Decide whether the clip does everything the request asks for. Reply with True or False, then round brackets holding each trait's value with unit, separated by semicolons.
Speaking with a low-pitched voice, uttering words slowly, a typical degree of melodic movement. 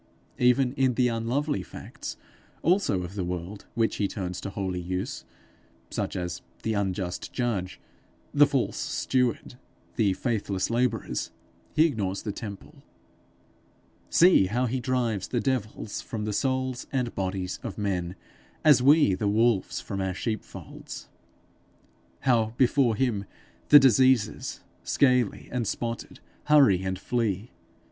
True (110 Hz; 130 wpm; 4.7 semitones)